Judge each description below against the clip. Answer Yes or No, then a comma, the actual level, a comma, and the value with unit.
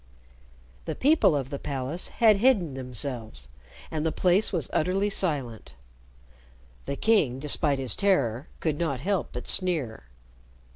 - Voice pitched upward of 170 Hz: No, medium, 150 Hz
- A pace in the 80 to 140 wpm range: Yes, slow, 135 wpm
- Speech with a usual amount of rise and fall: No, wide, 6.1 semitones